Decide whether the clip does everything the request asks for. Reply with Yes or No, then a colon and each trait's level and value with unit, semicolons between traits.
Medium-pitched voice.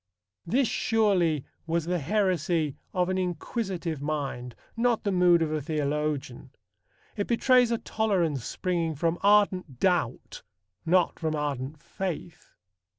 Yes: medium, 170 Hz